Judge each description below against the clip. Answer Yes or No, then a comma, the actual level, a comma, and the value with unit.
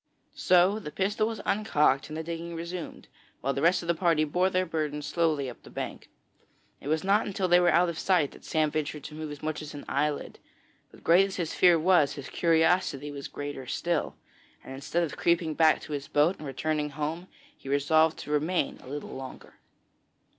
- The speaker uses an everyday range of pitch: Yes, average, 3.0 semitones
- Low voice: No, medium, 160 Hz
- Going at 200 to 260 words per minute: Yes, fast, 205 wpm